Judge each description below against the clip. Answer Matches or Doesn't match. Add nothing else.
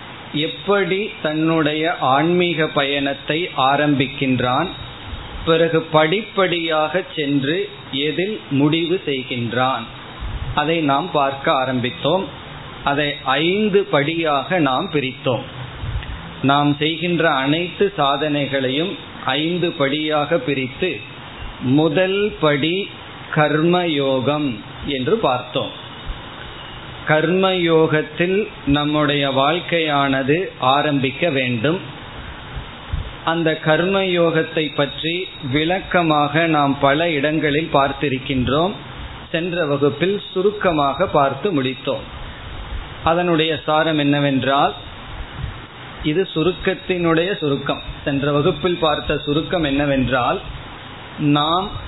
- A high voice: Doesn't match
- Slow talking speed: Matches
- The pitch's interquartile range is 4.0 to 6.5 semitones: Doesn't match